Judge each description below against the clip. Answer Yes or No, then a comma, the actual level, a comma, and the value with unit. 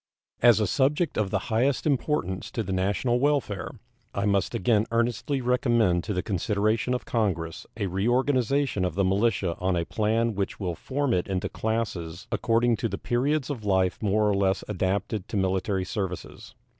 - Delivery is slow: No, average, 170 wpm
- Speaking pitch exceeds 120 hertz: No, low, 105 Hz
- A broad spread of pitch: No, average, 4.0 semitones